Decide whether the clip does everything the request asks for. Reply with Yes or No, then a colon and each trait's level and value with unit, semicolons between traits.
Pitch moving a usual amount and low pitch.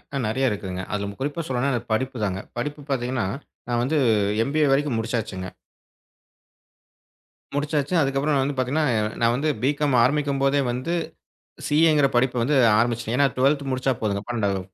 Yes: average, 3.7 semitones; low, 130 Hz